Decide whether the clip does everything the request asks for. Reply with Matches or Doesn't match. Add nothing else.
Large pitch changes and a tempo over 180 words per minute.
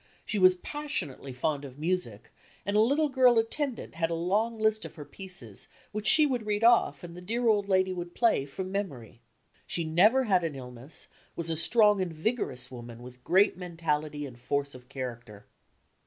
Matches